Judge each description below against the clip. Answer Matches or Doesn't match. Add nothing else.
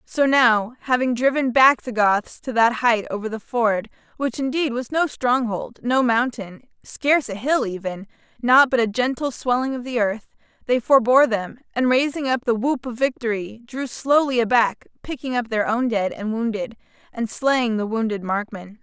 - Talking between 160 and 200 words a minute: Matches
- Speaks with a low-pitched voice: Doesn't match